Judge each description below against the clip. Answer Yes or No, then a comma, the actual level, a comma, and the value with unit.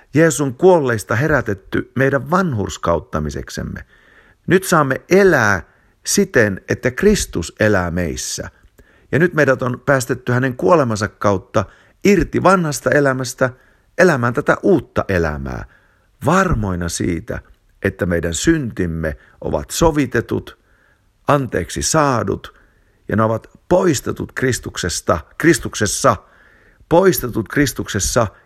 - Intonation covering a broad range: Yes, wide, 8.1 semitones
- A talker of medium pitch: No, low, 125 Hz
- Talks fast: No, slow, 95 wpm